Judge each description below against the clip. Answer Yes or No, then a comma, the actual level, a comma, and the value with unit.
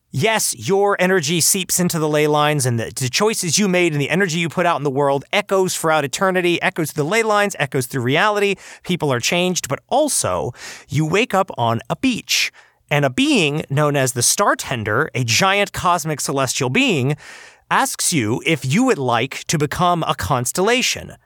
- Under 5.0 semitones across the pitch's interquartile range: No, average, 5.3 semitones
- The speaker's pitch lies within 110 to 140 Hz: No, medium, 160 Hz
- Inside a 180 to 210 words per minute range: Yes, average, 185 wpm